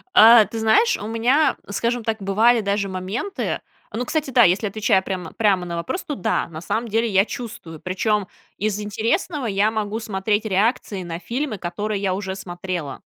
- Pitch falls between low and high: No, high, 210 Hz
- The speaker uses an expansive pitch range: No, average, 3.3 semitones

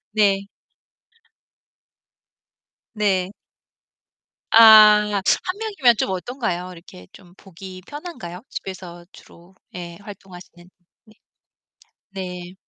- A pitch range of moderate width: Yes, average, 3.1 semitones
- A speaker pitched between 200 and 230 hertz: No, high, 190 Hz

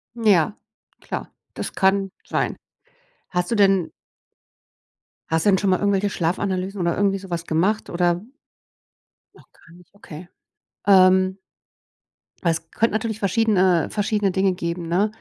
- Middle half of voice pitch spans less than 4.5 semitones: Yes, narrow, 2.5 semitones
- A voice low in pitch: No, high, 190 Hz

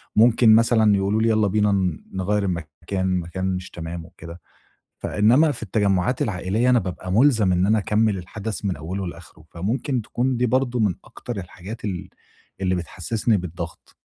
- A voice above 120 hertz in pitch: No, low, 100 Hz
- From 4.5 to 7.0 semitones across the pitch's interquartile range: No, average, 3.6 semitones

